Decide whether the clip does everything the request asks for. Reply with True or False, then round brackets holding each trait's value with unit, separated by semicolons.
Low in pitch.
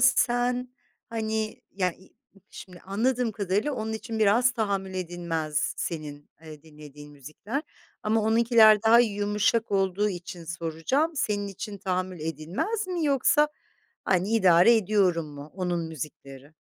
False (200 Hz)